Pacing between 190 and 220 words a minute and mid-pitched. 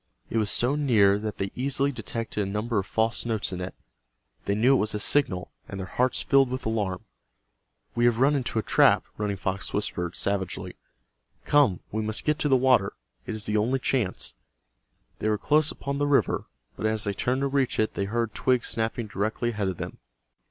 No: fast, 205 wpm; low, 110 Hz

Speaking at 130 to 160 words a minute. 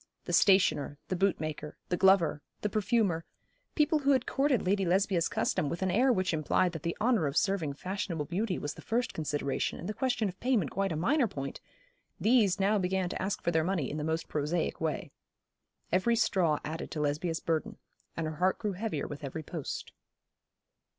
No: average, 190 wpm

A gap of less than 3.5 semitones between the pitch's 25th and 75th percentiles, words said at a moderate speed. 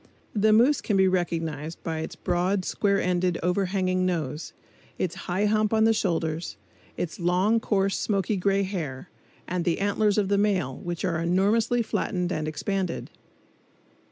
Yes: average, 2.9 semitones; average, 155 wpm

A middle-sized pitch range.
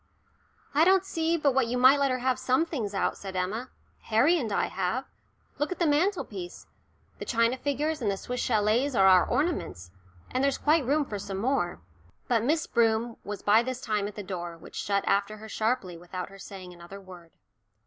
No: wide, 6.0 semitones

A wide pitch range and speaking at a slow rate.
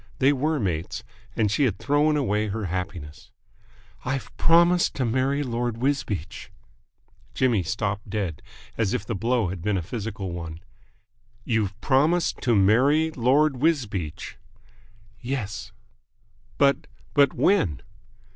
Yes: wide, 5.9 semitones; slow, 125 wpm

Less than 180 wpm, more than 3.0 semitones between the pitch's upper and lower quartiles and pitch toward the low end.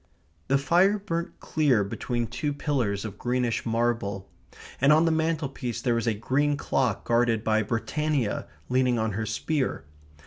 Yes: average, 150 wpm; average, 4.7 semitones; low, 125 Hz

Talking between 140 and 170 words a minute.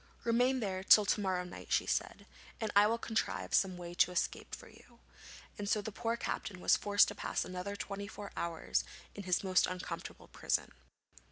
No: average, 190 wpm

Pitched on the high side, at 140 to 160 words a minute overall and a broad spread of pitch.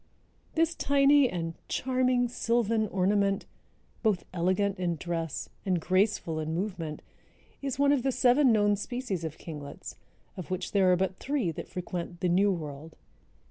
Yes: high, 195 Hz; average, 150 wpm; wide, 6.0 semitones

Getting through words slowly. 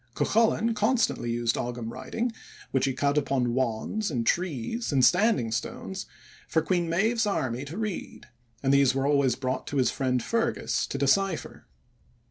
No: average, 155 wpm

